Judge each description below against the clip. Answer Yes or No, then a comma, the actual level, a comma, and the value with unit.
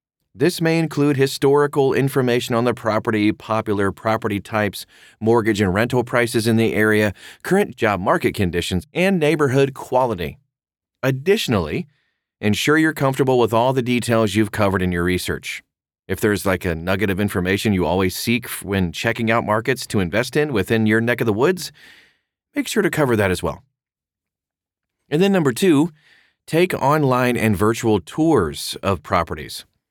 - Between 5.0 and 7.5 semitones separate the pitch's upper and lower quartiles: Yes, wide, 5.4 semitones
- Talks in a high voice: No, low, 115 Hz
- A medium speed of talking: Yes, average, 160 wpm